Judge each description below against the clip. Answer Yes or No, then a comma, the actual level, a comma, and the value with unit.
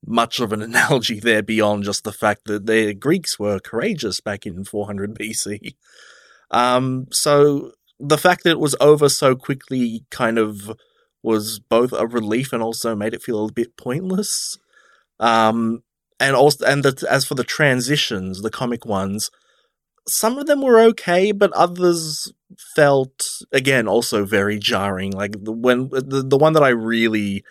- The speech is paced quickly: No, average, 165 wpm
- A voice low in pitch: Yes, low, 120 Hz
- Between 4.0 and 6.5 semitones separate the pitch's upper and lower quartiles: Yes, average, 5.0 semitones